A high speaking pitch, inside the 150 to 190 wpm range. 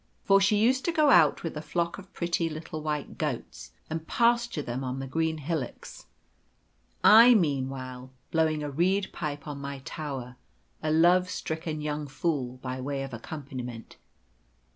No: medium, 155 Hz; average, 160 wpm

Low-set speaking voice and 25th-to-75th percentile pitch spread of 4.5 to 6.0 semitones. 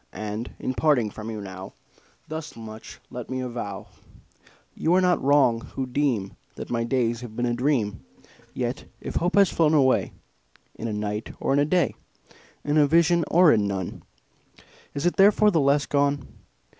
Yes: low, 130 Hz; average, 5.3 semitones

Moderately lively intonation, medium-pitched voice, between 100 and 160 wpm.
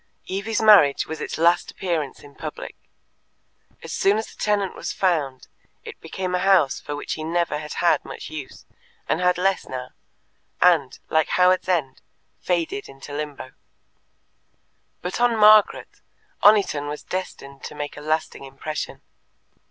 Yes: average, 4.3 semitones; medium, 165 Hz; average, 150 wpm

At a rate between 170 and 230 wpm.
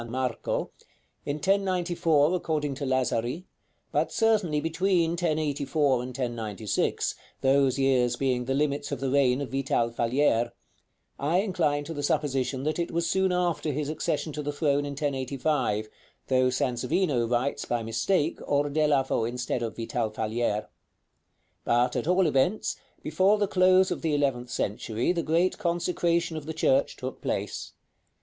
No: average, 145 wpm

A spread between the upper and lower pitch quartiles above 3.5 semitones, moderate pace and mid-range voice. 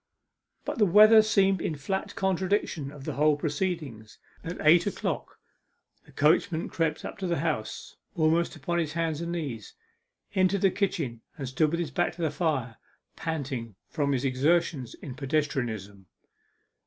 Yes: average, 4.1 semitones; average, 155 wpm; medium, 155 Hz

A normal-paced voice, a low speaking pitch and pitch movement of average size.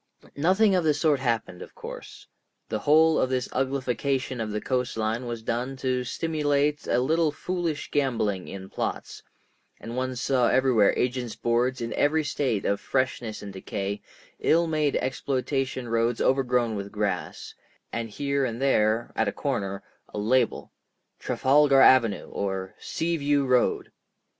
Yes: average, 150 wpm; low, 130 Hz; average, 3.8 semitones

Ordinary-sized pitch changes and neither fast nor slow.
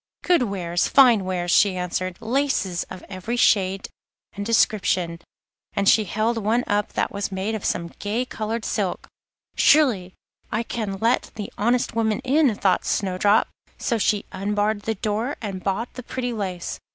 Yes: average, 3.4 semitones; average, 160 wpm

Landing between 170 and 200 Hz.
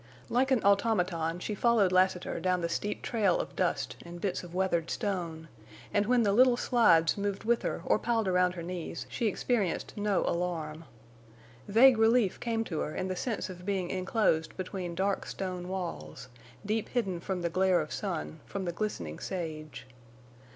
Yes: medium, 185 Hz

